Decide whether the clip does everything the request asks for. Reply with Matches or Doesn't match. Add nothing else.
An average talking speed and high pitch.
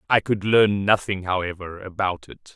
Doesn't match